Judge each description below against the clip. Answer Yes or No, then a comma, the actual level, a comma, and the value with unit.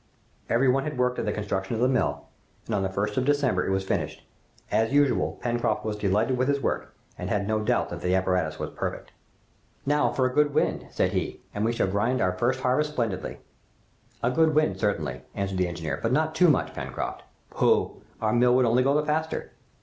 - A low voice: Yes, low, 120 Hz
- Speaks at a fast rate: Yes, fast, 215 wpm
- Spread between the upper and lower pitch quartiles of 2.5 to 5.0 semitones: No, wide, 5.4 semitones